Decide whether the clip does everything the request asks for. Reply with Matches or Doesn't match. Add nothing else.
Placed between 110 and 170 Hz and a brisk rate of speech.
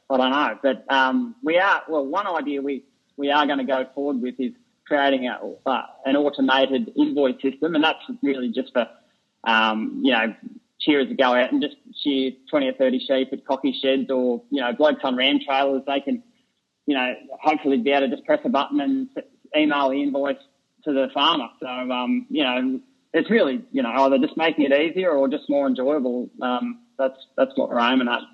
Matches